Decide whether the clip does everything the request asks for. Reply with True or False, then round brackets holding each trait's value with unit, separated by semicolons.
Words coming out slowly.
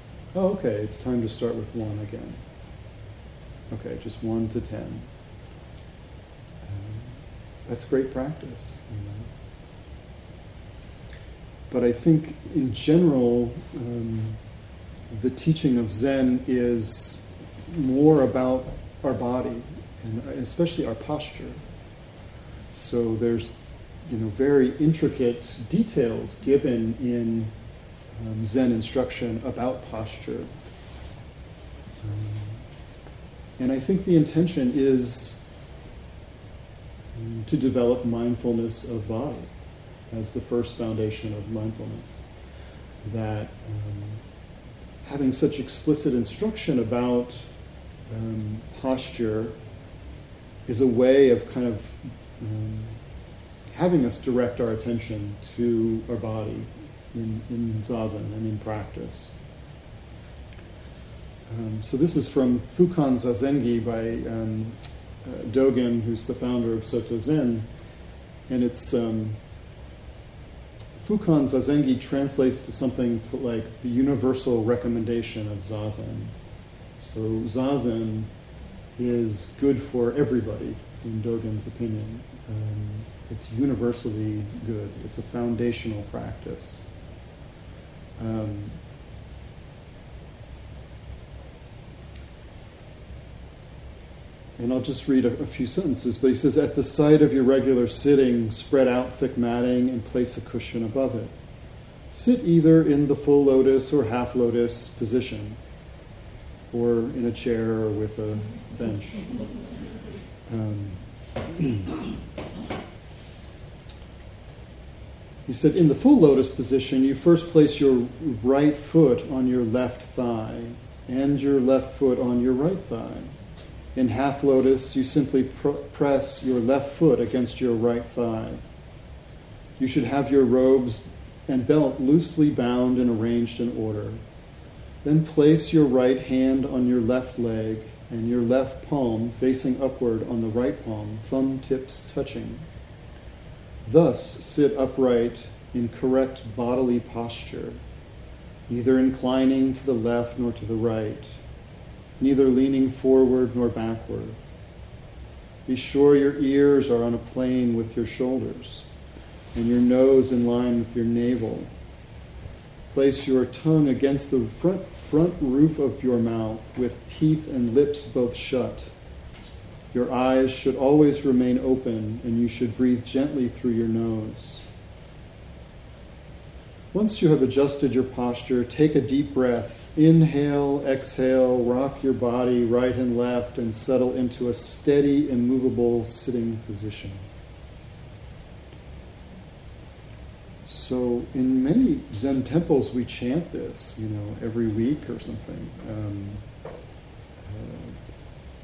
True (115 wpm)